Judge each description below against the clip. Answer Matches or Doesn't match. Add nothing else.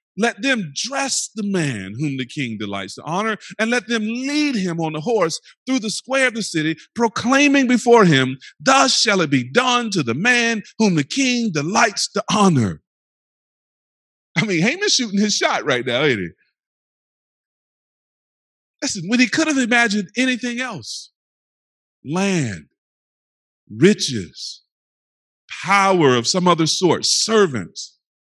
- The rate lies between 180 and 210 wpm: Doesn't match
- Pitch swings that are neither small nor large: Doesn't match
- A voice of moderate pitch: Doesn't match